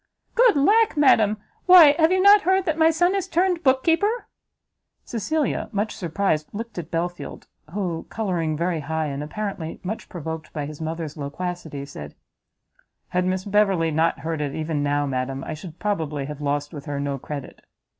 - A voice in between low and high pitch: Yes, medium, 175 Hz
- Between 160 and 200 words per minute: Yes, average, 175 wpm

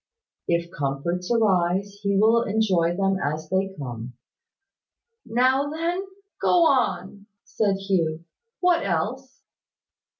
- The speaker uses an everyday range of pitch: No, wide, 5.7 semitones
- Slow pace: Yes, slow, 105 wpm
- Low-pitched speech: No, high, 195 Hz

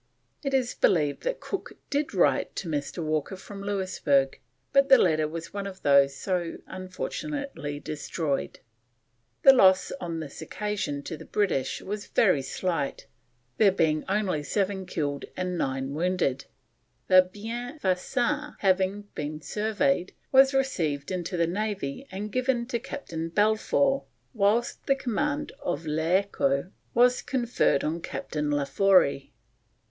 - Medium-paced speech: No, slow, 130 wpm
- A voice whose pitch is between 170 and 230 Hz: Yes, medium, 185 Hz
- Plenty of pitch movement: Yes, wide, 7.2 semitones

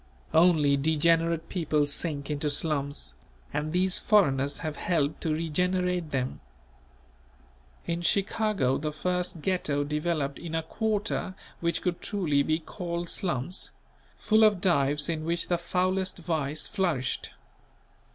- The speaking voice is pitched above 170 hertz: No, medium, 165 Hz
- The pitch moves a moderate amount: Yes, average, 3.5 semitones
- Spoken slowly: Yes, slow, 125 wpm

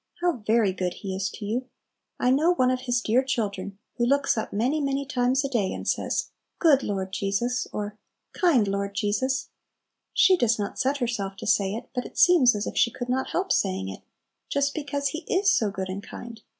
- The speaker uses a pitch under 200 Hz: No, high, 240 Hz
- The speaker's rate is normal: No, fast, 210 wpm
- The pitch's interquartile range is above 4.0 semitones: Yes, average, 5.2 semitones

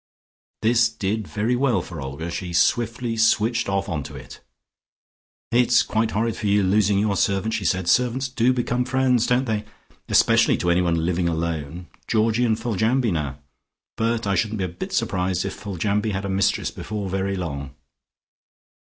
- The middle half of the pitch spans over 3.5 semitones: Yes, average, 4.2 semitones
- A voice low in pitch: Yes, low, 105 Hz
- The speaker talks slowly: No, average, 165 wpm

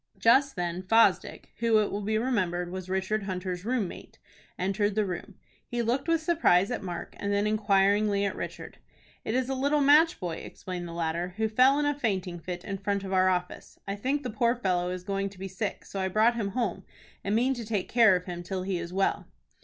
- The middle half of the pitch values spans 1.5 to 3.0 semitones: No, average, 4.0 semitones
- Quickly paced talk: Yes, fast, 225 wpm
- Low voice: No, high, 200 Hz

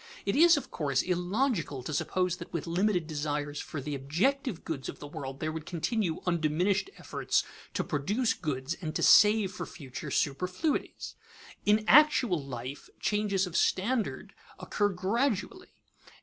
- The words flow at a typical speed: Yes, average, 150 wpm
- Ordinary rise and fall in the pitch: No, wide, 6.1 semitones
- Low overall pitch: No, medium, 180 Hz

